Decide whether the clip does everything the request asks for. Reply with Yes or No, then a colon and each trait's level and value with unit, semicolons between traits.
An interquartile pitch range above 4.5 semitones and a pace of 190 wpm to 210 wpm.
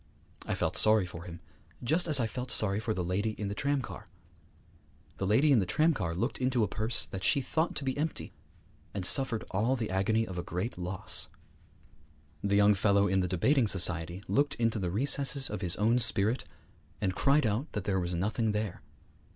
Yes: average, 5.1 semitones; average, 195 wpm